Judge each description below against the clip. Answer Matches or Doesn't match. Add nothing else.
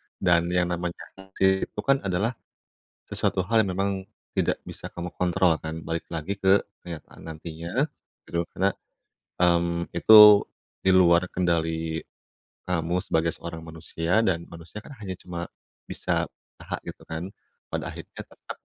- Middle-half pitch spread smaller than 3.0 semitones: Matches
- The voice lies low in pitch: Matches